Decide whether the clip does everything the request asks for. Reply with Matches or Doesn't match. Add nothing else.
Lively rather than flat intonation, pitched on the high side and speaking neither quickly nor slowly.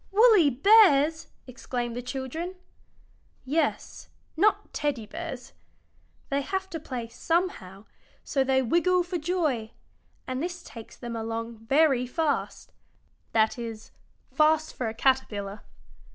Doesn't match